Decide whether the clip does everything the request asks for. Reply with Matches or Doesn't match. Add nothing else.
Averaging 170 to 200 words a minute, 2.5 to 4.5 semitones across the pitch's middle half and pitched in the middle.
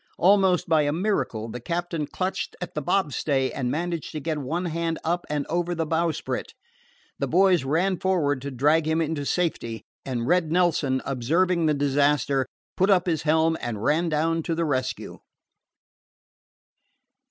Doesn't match